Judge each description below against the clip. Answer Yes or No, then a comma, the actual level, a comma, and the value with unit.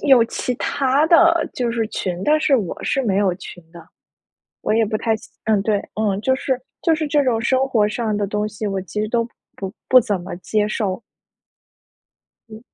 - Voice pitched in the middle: No, high, 220 Hz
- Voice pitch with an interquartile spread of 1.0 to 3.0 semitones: No, average, 4.3 semitones